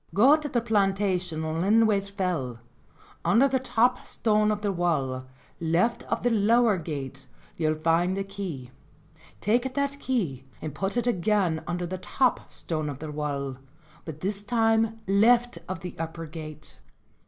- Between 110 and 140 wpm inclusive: No, average, 155 wpm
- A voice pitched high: Yes, high, 195 Hz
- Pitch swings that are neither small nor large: No, wide, 5.9 semitones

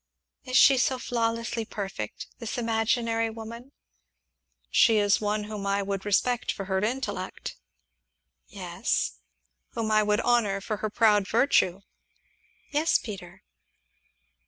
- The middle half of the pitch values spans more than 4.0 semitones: No, narrow, 2.6 semitones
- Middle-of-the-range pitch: No, high, 215 Hz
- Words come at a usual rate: No, slow, 120 wpm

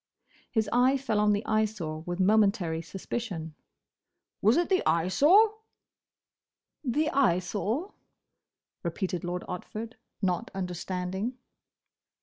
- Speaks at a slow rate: Yes, slow, 100 wpm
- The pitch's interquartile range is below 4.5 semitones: No, average, 5.2 semitones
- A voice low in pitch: No, high, 205 Hz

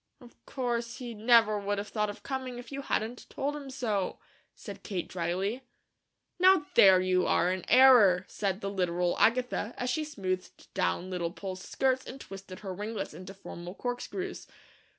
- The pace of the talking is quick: No, average, 170 wpm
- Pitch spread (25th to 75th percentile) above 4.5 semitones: Yes, average, 5.1 semitones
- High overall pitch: Yes, high, 210 Hz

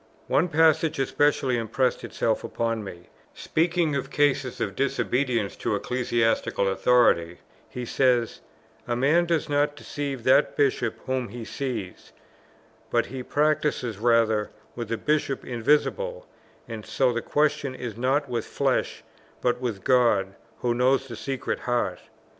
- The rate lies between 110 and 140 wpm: Yes, slow, 135 wpm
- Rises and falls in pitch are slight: No, average, 3.8 semitones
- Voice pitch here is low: Yes, low, 125 Hz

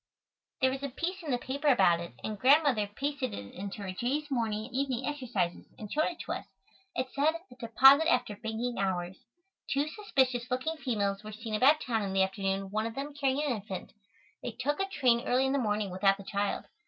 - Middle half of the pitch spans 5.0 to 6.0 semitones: Yes, average, 5.3 semitones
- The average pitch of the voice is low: No, high, 245 Hz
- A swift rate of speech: Yes, fast, 215 wpm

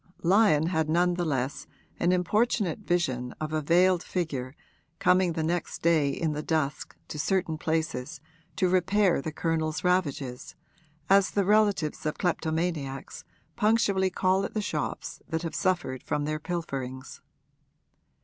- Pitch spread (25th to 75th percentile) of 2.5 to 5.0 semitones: Yes, average, 3.4 semitones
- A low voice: No, medium, 165 Hz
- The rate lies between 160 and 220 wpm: No, average, 140 wpm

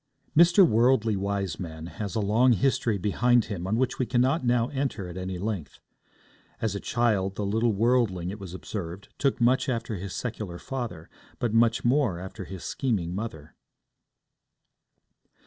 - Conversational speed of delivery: Yes, average, 155 wpm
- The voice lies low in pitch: Yes, low, 110 Hz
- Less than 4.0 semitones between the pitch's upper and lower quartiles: No, average, 4.4 semitones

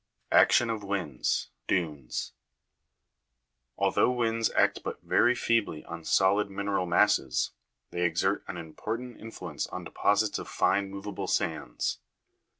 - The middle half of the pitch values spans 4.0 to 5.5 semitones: Yes, average, 4.3 semitones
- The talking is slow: Yes, slow, 125 wpm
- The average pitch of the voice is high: No, low, 100 Hz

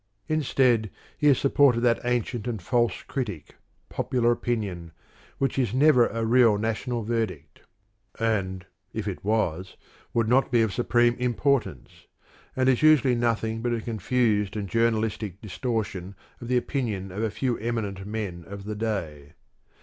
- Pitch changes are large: No, average, 3.2 semitones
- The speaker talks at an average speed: Yes, average, 150 wpm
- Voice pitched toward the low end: Yes, low, 115 Hz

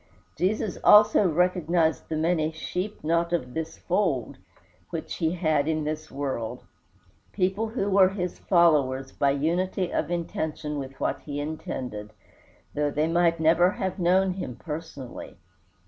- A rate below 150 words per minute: Yes, average, 140 wpm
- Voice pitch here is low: No, medium, 165 Hz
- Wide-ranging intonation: No, average, 3.5 semitones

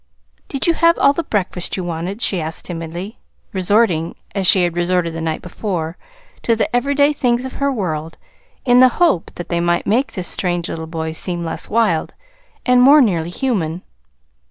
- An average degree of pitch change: No, wide, 6.5 semitones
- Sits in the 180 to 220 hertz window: Yes, medium, 185 Hz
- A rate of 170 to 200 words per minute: Yes, average, 180 wpm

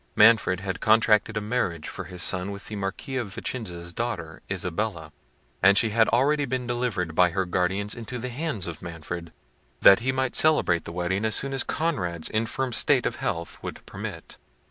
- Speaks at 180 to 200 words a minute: Yes, average, 185 wpm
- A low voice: Yes, low, 100 Hz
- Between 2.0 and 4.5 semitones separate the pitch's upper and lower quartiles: No, average, 5.3 semitones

